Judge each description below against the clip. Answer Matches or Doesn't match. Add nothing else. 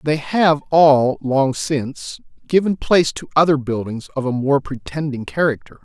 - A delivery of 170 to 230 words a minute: Doesn't match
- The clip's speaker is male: Matches